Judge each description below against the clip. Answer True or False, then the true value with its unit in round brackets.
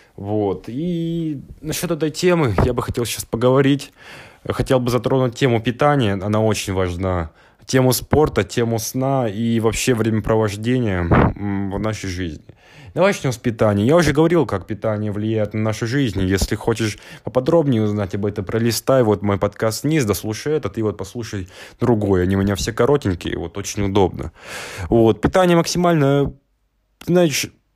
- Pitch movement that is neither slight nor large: True (4.7 semitones)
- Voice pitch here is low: True (115 Hz)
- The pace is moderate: True (150 wpm)